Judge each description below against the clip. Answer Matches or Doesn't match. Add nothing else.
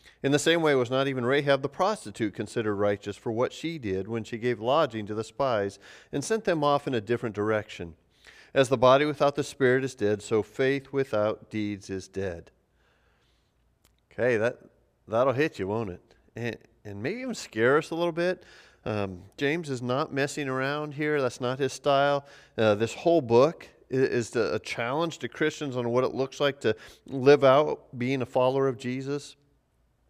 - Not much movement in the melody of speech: Doesn't match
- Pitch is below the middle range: Matches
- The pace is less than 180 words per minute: Doesn't match